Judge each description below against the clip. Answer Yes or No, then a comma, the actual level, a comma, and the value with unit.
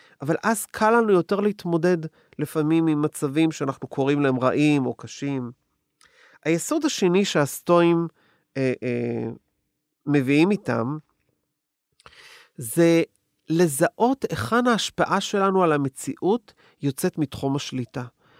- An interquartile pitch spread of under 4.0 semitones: No, average, 4.9 semitones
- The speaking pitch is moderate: Yes, medium, 160 Hz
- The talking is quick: No, average, 105 wpm